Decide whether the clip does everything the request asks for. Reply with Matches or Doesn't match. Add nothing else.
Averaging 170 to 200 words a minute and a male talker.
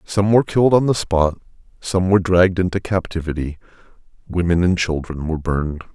Doesn't match